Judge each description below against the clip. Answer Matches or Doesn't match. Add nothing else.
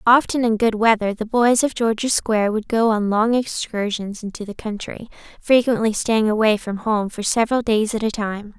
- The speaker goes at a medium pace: Matches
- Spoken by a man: Doesn't match